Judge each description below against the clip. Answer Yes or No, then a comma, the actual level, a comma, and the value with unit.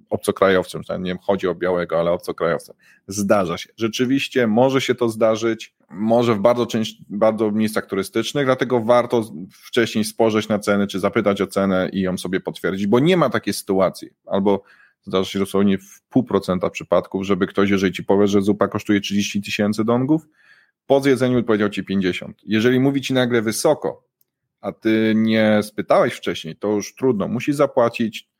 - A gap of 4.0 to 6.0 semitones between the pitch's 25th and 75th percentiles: No, average, 3.3 semitones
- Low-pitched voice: Yes, low, 110 Hz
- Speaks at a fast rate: Yes, fast, 170 wpm